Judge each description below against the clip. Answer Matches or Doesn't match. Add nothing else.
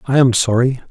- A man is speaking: Matches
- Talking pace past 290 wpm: Doesn't match